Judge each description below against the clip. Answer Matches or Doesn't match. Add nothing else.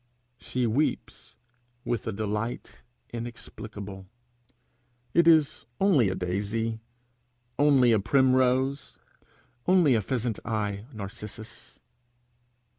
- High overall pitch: Doesn't match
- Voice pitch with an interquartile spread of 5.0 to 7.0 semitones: Doesn't match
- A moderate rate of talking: Doesn't match